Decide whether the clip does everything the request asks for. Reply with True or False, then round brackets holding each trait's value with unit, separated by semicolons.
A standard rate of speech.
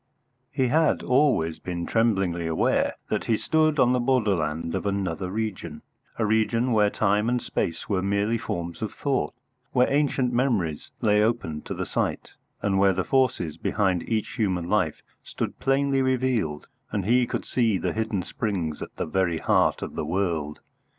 True (170 wpm)